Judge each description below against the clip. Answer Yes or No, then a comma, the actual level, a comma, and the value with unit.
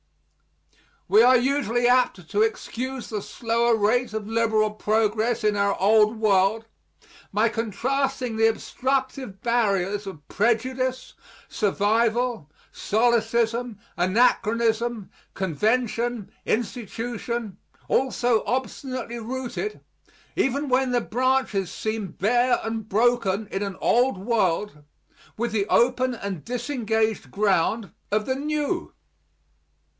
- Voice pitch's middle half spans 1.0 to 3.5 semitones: Yes, average, 2.9 semitones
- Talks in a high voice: Yes, high, 225 Hz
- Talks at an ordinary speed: No, slow, 105 wpm